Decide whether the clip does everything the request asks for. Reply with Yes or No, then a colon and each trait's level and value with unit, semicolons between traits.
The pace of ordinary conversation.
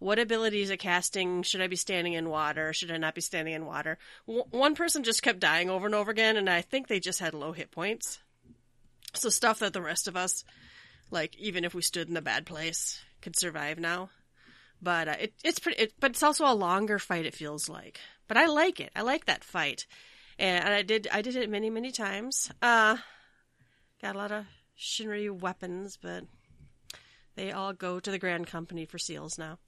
No: fast, 215 wpm